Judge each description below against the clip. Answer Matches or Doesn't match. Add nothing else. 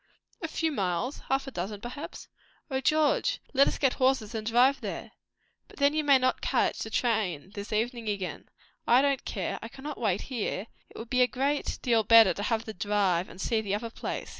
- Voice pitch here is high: Matches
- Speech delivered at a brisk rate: Matches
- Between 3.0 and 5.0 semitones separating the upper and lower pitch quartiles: Matches